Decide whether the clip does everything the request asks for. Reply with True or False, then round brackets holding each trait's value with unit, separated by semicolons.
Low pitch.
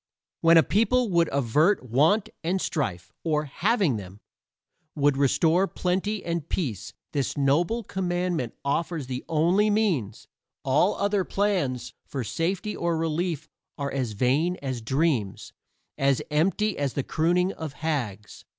False (160 Hz)